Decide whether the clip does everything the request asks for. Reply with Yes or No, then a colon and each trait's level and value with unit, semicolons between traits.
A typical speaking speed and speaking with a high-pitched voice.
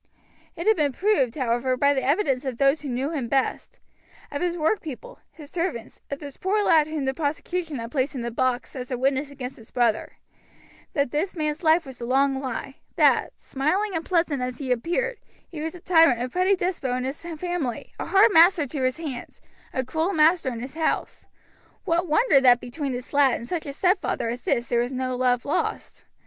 No: fast, 210 wpm; very high, 280 Hz